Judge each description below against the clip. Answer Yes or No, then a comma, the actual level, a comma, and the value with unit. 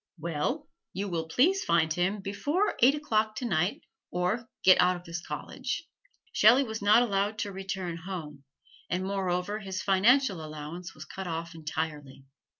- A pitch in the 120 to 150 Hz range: No, high, 190 Hz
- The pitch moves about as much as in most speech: Yes, average, 4.4 semitones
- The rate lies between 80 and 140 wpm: No, average, 155 wpm